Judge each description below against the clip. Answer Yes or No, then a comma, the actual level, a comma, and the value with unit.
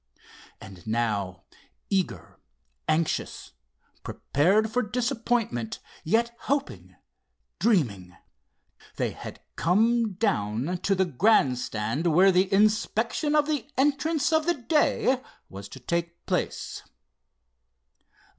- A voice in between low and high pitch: No, high, 195 Hz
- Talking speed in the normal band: No, slow, 100 wpm